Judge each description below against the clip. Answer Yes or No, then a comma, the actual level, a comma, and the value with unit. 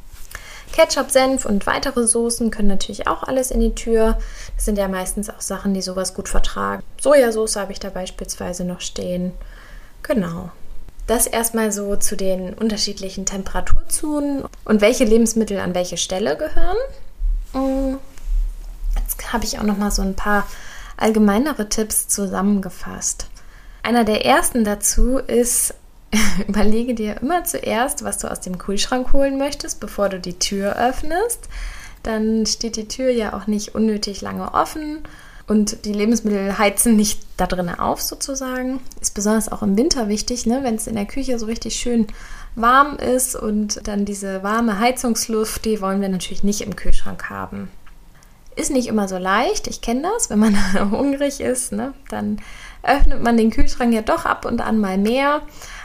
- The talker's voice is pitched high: Yes, high, 220 Hz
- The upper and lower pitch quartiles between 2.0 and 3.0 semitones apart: No, average, 3.7 semitones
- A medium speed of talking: Yes, average, 160 wpm